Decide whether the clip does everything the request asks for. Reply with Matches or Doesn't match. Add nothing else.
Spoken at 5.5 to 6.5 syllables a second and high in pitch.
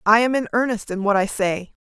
Matches